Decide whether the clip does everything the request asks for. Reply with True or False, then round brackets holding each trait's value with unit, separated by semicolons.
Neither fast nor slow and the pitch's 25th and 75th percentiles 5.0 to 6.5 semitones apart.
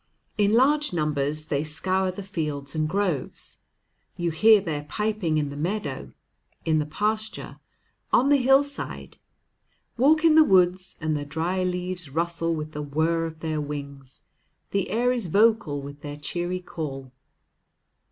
True (150 wpm; 5.4 semitones)